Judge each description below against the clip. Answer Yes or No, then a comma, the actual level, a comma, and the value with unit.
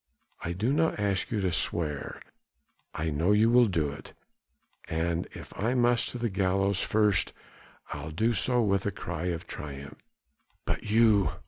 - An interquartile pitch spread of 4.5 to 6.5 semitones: Yes, average, 5.1 semitones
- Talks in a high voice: No, low, 100 Hz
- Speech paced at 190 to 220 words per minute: No, average, 150 wpm